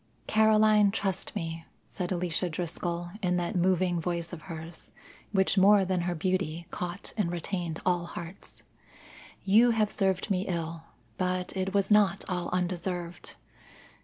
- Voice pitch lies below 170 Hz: No, medium, 180 Hz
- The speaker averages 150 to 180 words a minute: No, average, 140 wpm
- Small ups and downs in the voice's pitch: Yes, narrow, 2.0 semitones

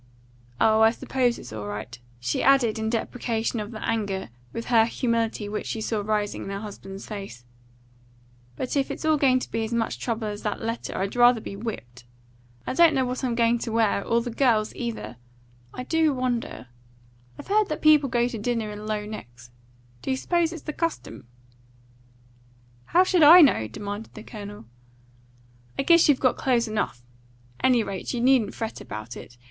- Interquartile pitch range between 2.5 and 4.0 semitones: Yes, average, 3.6 semitones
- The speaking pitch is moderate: No, high, 230 Hz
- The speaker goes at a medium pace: Yes, average, 185 wpm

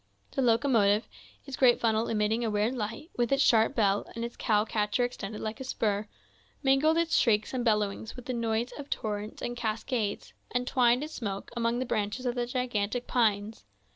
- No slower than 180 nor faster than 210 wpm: Yes, average, 190 wpm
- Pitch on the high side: Yes, high, 230 Hz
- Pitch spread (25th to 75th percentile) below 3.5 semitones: Yes, average, 2.9 semitones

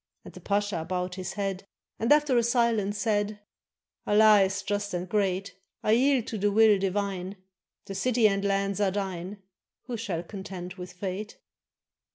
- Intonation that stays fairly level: Yes, narrow, 2.1 semitones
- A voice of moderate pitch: No, high, 200 Hz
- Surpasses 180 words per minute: No, average, 165 wpm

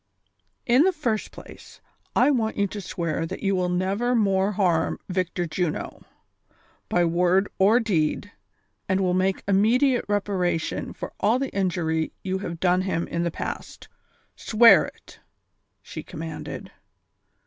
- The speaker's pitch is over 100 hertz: Yes, high, 190 Hz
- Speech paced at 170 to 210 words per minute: No, average, 150 wpm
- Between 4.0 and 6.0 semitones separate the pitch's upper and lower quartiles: No, average, 3.1 semitones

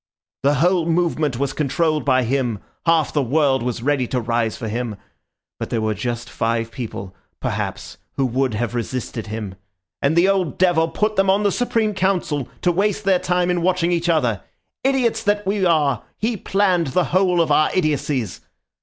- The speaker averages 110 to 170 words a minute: No, average, 180 wpm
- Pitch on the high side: No, medium, 155 Hz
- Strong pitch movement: Yes, wide, 6.9 semitones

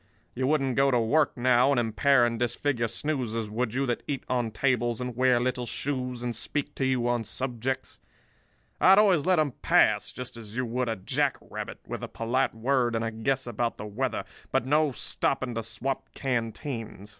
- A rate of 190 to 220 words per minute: Yes, average, 195 wpm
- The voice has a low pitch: Yes, low, 125 Hz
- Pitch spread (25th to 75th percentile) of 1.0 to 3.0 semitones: Yes, average, 2.7 semitones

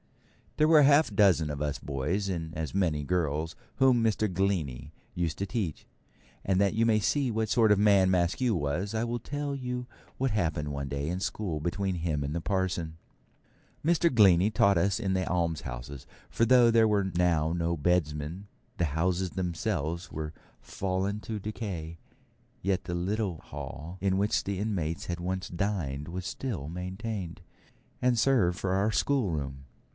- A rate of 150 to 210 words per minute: Yes, average, 170 wpm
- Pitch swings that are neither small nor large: Yes, average, 4.6 semitones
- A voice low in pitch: Yes, very low, 95 Hz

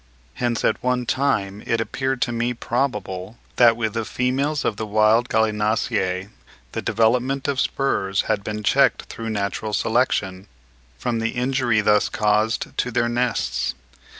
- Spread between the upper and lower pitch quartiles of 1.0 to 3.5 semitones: Yes, average, 2.8 semitones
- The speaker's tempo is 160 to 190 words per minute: No, average, 150 wpm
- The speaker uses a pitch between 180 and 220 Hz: No, low, 115 Hz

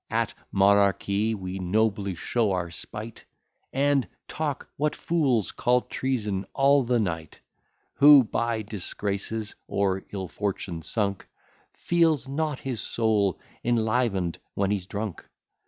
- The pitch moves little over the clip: No, average, 4.5 semitones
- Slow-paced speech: Yes, slow, 120 wpm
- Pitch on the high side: No, low, 110 Hz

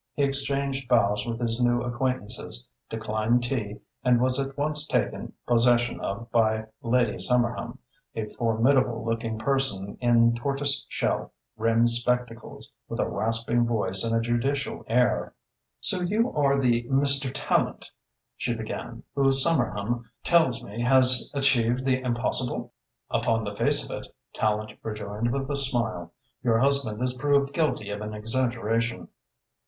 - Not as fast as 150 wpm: Yes, average, 140 wpm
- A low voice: Yes, low, 120 Hz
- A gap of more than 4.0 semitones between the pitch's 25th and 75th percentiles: No, average, 2.9 semitones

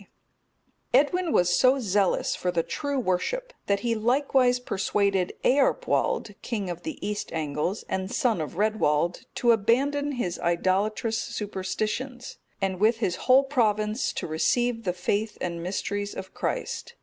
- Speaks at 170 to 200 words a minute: No, average, 145 wpm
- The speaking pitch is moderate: No, high, 215 Hz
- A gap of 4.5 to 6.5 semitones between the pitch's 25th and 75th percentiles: Yes, average, 5.2 semitones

